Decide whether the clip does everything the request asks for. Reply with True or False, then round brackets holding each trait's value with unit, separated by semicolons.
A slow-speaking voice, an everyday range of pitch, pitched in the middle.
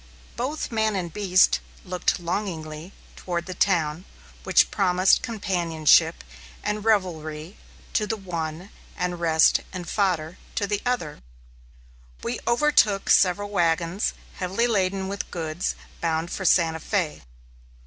True (120 wpm; 3.6 semitones; 180 Hz)